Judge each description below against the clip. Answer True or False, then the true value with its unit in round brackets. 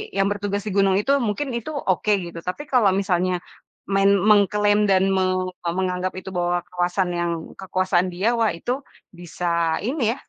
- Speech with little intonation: True (2.3 semitones)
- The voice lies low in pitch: False (190 Hz)